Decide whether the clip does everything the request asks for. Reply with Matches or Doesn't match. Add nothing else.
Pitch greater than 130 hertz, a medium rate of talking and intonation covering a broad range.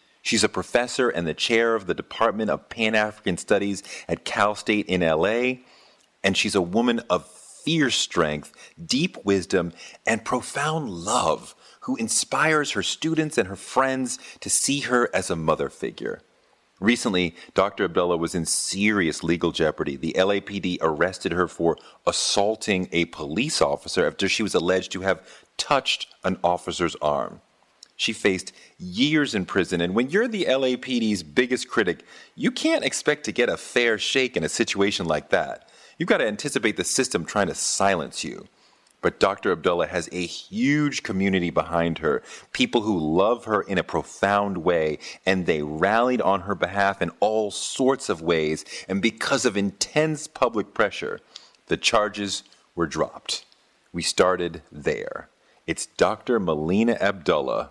Doesn't match